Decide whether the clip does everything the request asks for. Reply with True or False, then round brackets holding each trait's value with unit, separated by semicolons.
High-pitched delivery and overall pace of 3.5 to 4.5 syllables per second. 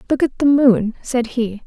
True (245 Hz; 4.4 syllables/s)